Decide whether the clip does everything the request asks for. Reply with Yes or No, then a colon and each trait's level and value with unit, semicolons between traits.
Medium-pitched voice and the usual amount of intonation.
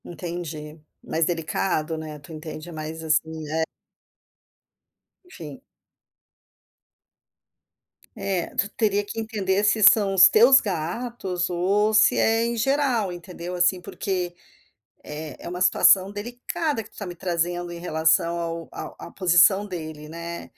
Yes: medium, 175 Hz; average, 4.0 semitones